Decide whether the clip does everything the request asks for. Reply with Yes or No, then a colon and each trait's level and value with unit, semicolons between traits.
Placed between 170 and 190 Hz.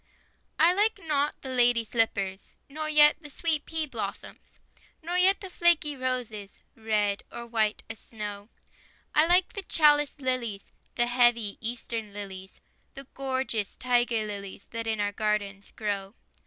No: high, 240 Hz